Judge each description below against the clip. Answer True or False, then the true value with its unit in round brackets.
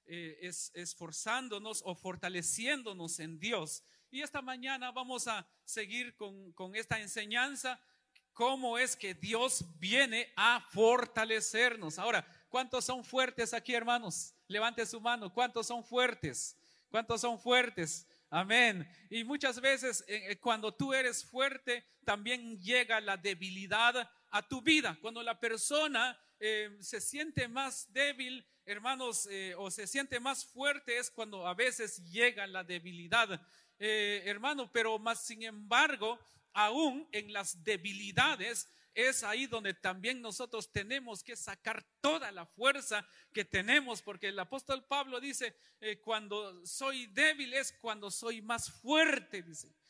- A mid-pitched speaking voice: False (230 Hz)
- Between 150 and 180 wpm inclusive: False (135 wpm)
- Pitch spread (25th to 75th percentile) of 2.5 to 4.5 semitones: True (4.0 semitones)